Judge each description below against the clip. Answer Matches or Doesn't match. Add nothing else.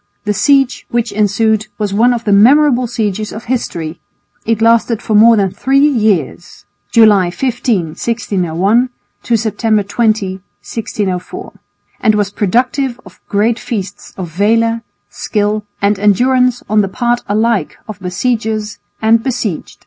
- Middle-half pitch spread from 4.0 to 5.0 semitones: Doesn't match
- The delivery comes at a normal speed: Doesn't match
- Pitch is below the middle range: Doesn't match